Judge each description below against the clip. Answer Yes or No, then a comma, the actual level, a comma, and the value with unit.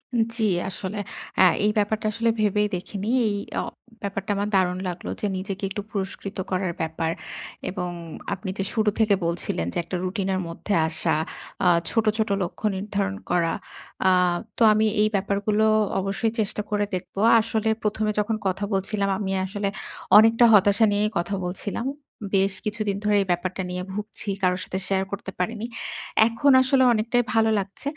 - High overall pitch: Yes, high, 200 Hz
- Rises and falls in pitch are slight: Yes, narrow, 2.3 semitones